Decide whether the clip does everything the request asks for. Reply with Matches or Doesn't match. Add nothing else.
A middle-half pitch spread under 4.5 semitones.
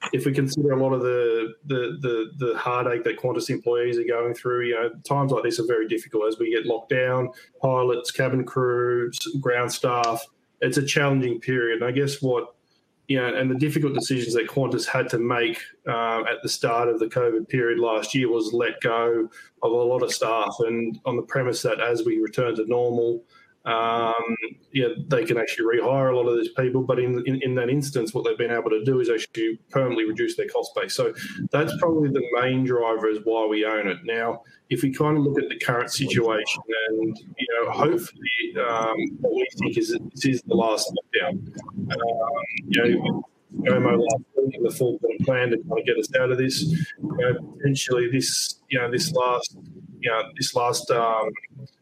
Doesn't match